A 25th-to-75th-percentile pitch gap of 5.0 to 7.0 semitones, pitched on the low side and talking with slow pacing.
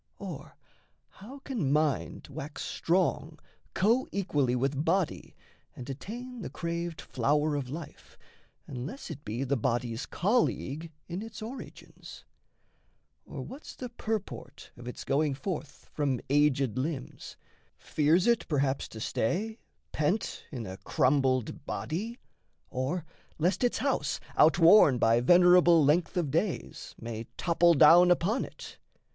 No: wide, 5.6 semitones; medium, 155 Hz; slow, 125 wpm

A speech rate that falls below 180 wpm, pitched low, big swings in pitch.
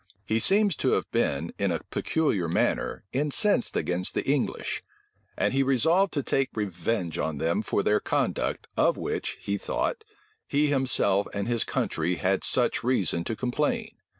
Yes: average, 160 wpm; low, 115 Hz; wide, 7.6 semitones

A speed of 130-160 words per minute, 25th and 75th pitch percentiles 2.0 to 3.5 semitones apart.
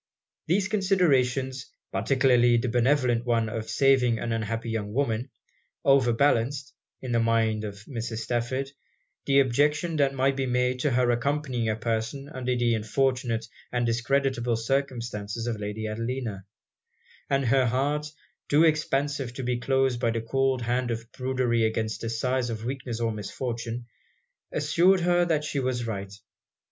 Yes: average, 150 wpm; average, 3.0 semitones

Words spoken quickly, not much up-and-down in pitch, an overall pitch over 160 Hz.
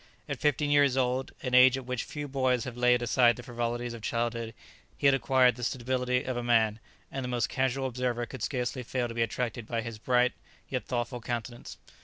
No: fast, 210 wpm; narrow, 1.6 semitones; low, 125 Hz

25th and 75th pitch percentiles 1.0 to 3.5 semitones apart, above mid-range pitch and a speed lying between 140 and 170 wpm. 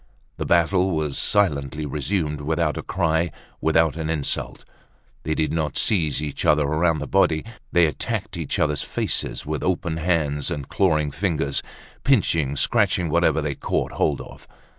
No: narrow, 2.4 semitones; very low, 80 Hz; average, 155 wpm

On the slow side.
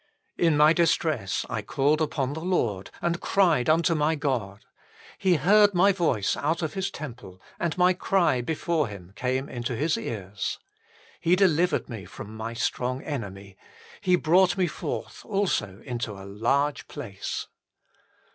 No: average, 155 wpm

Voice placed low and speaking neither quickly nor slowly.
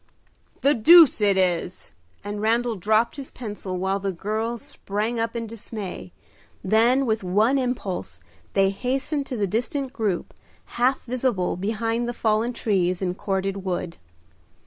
No: high, 220 Hz; average, 145 wpm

